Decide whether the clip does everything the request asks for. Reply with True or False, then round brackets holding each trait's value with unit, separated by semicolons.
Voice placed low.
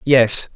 True (125 Hz)